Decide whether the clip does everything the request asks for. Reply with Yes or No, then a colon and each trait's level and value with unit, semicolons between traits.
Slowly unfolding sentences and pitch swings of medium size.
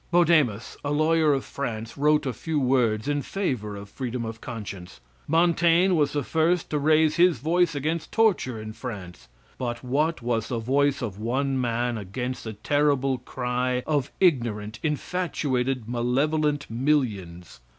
No: average, 150 wpm; average, 4.8 semitones